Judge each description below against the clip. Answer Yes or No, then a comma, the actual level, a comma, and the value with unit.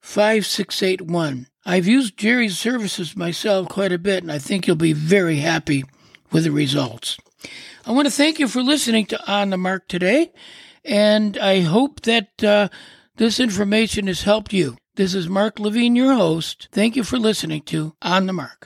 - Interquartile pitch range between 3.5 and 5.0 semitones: Yes, average, 4.2 semitones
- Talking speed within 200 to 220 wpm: No, average, 175 wpm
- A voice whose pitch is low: No, high, 200 Hz